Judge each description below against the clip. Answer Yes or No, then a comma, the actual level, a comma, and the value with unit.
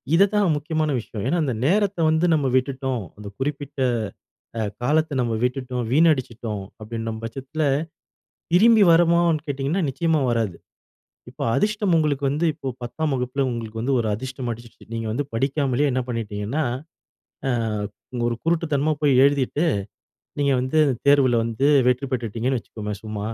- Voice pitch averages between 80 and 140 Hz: Yes, low, 135 Hz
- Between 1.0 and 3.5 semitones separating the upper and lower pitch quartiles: No, average, 4.8 semitones